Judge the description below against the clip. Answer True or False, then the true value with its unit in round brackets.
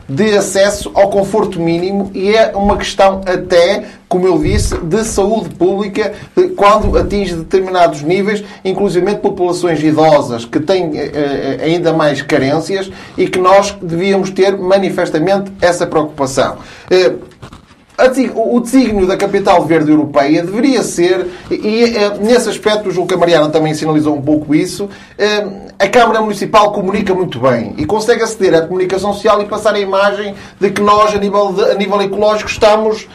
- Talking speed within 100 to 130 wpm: False (150 wpm)